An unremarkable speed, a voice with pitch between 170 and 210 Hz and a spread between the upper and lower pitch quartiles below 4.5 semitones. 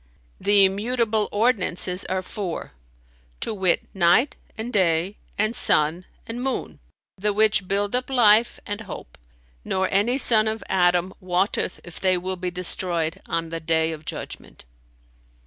Yes: average, 145 wpm; high, 190 Hz; average, 3.4 semitones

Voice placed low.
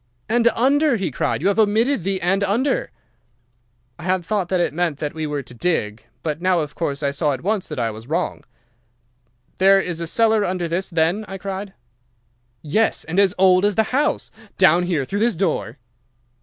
No: medium, 185 Hz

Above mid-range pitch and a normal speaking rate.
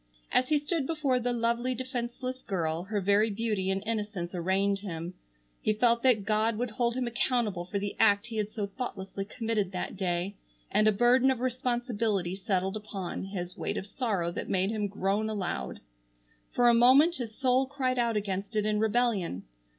Yes: high, 215 Hz; average, 180 wpm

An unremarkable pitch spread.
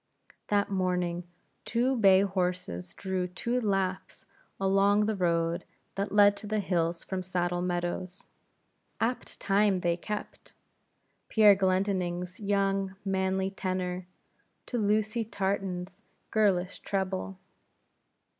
No: narrow, 2.1 semitones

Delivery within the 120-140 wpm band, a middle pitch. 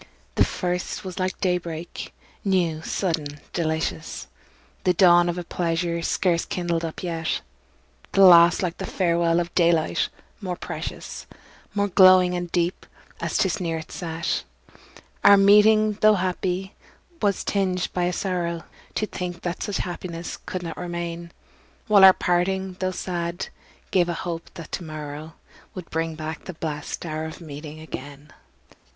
No: average, 150 wpm; medium, 175 Hz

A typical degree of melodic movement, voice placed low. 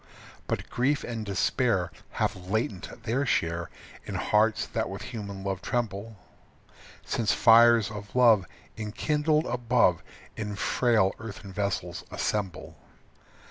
Yes: average, 3.3 semitones; low, 110 Hz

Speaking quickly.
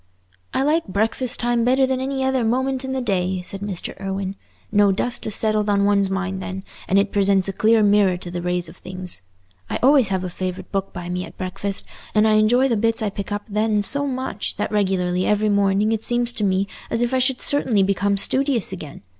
Yes: fast, 220 wpm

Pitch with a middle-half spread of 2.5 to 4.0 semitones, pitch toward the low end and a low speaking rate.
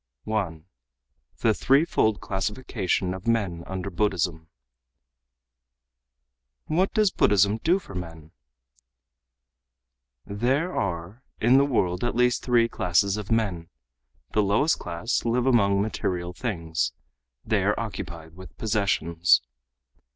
No: average, 5.1 semitones; low, 100 Hz; slow, 110 wpm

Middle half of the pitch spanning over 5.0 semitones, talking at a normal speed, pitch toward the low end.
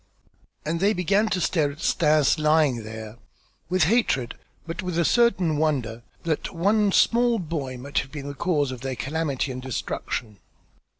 No: wide, 5.4 semitones; average, 165 wpm; medium, 155 Hz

